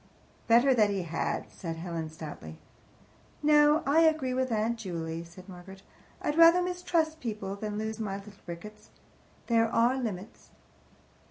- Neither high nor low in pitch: No, high, 215 Hz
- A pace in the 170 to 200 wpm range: No, average, 145 wpm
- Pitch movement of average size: No, wide, 6.6 semitones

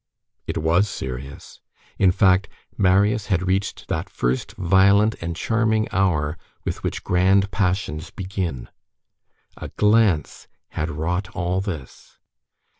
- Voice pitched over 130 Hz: No, very low, 95 Hz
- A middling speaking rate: No, slow, 115 wpm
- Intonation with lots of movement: No, average, 3.3 semitones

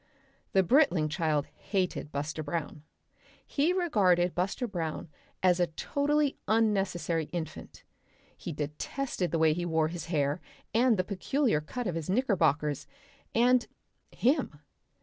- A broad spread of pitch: Yes, wide, 6.7 semitones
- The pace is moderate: No, slow, 130 wpm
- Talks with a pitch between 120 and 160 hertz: No, medium, 180 Hz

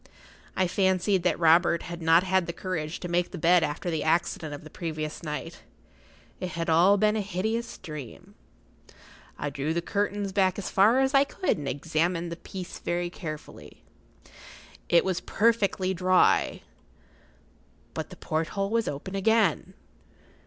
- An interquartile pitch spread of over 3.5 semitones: No, average, 3.2 semitones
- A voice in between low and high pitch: Yes, medium, 175 Hz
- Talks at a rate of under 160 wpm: Yes, average, 150 wpm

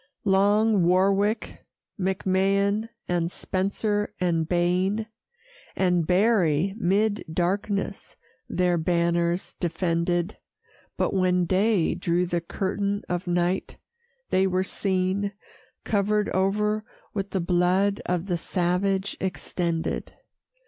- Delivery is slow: Yes, slow, 100 wpm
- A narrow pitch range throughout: Yes, narrow, 2.3 semitones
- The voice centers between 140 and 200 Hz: Yes, medium, 185 Hz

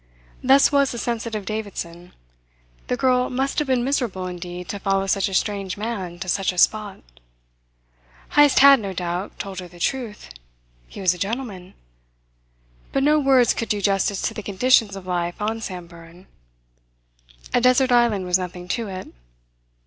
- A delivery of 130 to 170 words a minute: Yes, average, 165 wpm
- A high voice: Yes, high, 200 Hz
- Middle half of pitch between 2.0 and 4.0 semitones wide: No, average, 5.1 semitones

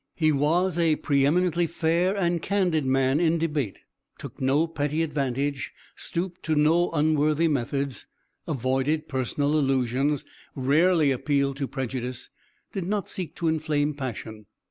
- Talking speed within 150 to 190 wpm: No, slow, 135 wpm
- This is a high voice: No, medium, 150 Hz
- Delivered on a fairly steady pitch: No, average, 3.5 semitones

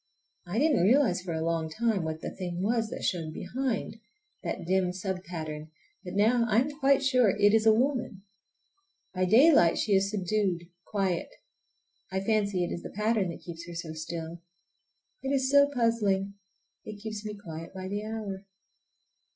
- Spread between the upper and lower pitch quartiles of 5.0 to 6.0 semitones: No, average, 4.2 semitones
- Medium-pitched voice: No, high, 200 Hz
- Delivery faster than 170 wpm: No, average, 165 wpm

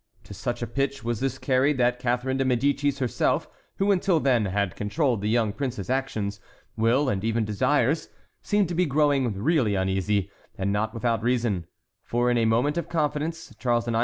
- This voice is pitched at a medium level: No, low, 120 Hz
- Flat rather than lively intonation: No, average, 4.3 semitones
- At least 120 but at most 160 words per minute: No, average, 185 wpm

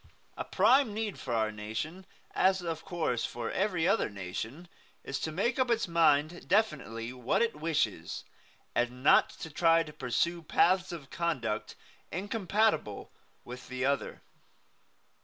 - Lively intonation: Yes, wide, 7.2 semitones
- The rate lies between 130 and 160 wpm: Yes, average, 145 wpm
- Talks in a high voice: No, medium, 160 Hz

